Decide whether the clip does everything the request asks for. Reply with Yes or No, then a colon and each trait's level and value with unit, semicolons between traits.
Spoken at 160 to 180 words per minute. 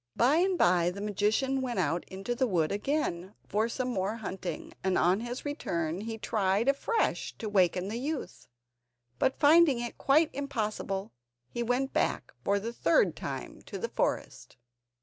Yes: average, 165 wpm